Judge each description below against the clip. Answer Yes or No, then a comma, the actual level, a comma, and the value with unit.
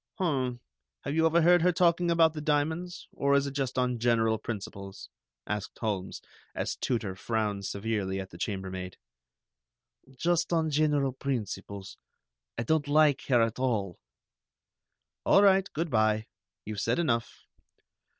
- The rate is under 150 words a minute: Yes, average, 140 wpm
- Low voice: Yes, low, 130 Hz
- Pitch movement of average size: No, wide, 6.8 semitones